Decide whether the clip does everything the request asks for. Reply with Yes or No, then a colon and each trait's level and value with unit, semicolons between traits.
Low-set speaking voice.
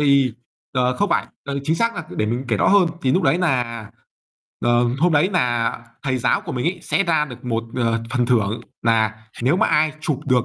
Yes: low, 130 Hz